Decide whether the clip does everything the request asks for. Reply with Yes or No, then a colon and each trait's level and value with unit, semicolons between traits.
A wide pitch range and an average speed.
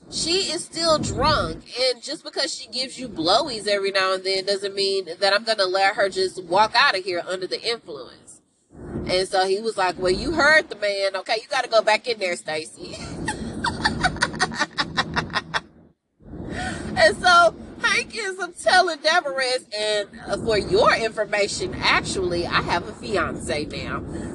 Yes: wide, 7.9 semitones; average, 160 wpm